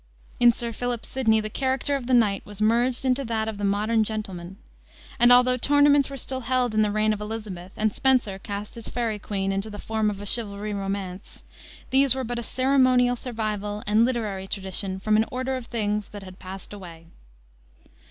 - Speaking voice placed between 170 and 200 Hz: No, high, 220 Hz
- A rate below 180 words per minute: No, average, 195 wpm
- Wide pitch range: No, average, 3.4 semitones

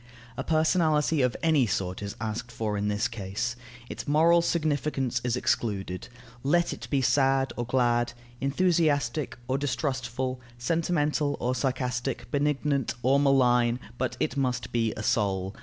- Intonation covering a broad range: No, average, 3.5 semitones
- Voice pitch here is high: No, low, 130 Hz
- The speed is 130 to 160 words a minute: Yes, average, 140 wpm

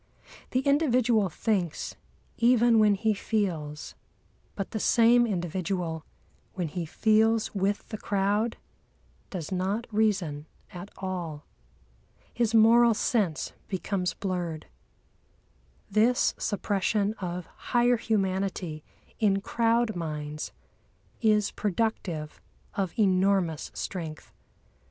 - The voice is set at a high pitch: Yes, high, 200 Hz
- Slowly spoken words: Yes, slow, 95 wpm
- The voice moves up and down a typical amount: Yes, average, 4.0 semitones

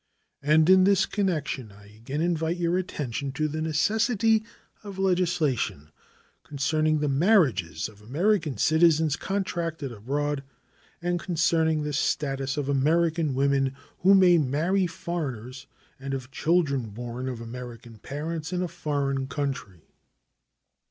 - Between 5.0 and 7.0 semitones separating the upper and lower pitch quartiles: No, average, 4.4 semitones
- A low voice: No, medium, 150 Hz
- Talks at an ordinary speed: No, slow, 125 wpm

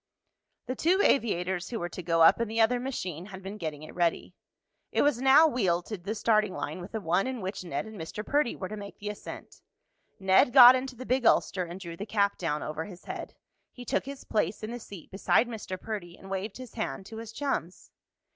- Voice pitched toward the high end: Yes, high, 205 Hz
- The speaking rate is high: Yes, fast, 230 wpm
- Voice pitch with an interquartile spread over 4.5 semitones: Yes, average, 5.0 semitones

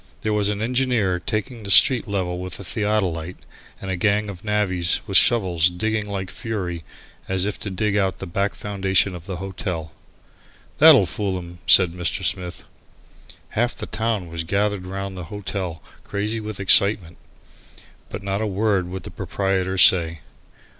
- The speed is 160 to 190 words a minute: Yes, average, 165 wpm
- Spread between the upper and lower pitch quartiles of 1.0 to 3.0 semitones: Yes, average, 2.7 semitones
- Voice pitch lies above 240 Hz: No, very low, 95 Hz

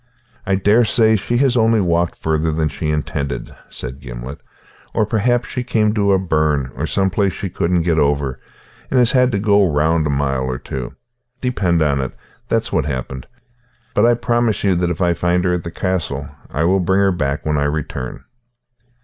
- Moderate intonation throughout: No, wide, 6.1 semitones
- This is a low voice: Yes, very low, 85 Hz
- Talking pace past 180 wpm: Yes, average, 190 wpm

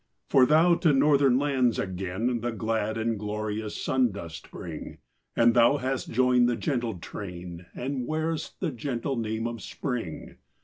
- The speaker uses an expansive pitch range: No, average, 3.8 semitones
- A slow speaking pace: No, average, 150 wpm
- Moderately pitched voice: No, low, 120 Hz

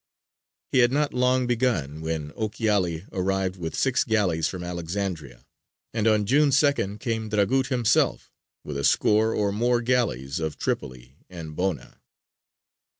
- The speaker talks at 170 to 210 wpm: No, average, 140 wpm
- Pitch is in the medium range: No, low, 100 Hz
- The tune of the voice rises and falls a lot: Yes, wide, 6.8 semitones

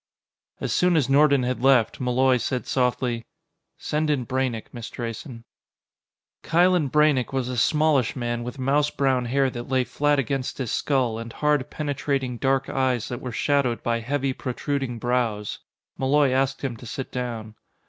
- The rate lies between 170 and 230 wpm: No, average, 160 wpm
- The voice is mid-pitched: No, low, 130 Hz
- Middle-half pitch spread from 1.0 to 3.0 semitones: Yes, narrow, 2.5 semitones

